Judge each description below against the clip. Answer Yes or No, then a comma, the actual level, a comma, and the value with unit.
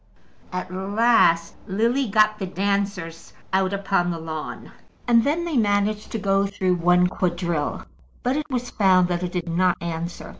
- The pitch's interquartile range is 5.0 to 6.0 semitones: No, average, 3.4 semitones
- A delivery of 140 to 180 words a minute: Yes, average, 160 wpm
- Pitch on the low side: No, high, 190 Hz